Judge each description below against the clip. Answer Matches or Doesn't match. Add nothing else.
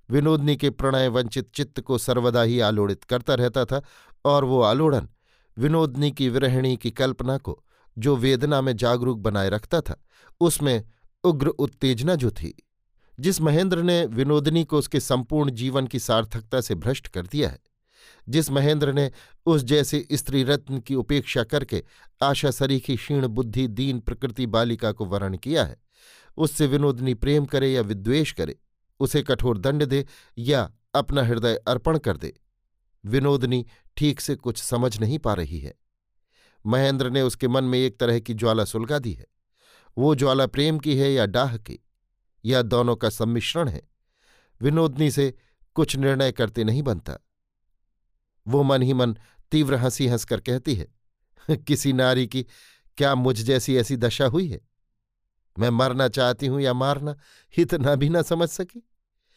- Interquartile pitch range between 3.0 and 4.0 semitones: Matches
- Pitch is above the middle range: Doesn't match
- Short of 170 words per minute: Matches